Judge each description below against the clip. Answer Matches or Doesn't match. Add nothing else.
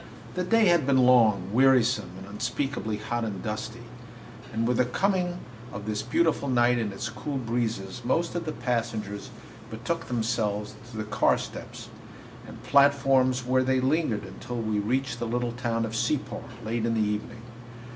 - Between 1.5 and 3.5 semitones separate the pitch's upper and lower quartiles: Matches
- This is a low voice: Matches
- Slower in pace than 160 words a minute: Doesn't match